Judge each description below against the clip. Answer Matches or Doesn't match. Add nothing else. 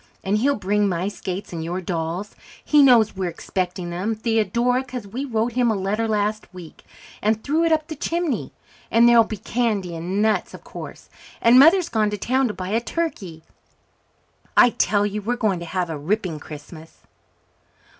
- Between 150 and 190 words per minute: Matches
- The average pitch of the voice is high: Matches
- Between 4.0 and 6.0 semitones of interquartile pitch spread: Matches